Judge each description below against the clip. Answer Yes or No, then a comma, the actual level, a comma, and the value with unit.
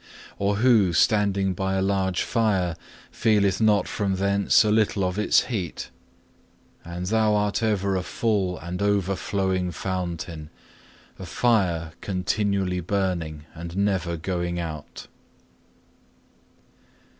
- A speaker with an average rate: No, slow, 115 wpm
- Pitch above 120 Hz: No, very low, 95 Hz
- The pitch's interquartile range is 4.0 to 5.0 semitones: No, narrow, 2.5 semitones